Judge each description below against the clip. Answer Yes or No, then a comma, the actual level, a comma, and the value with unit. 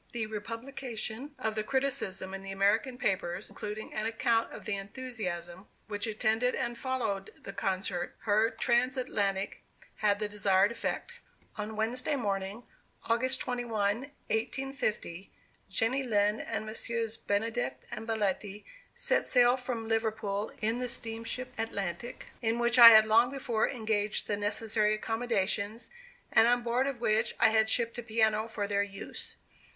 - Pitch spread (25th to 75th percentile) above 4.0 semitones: No, narrow, 2.6 semitones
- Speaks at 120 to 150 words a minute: Yes, average, 145 wpm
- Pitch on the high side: Yes, high, 220 Hz